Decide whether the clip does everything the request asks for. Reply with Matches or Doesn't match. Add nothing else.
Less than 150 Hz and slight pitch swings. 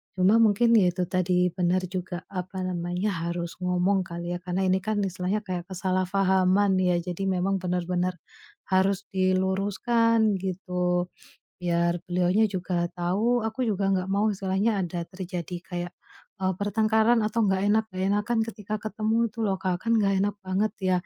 Doesn't match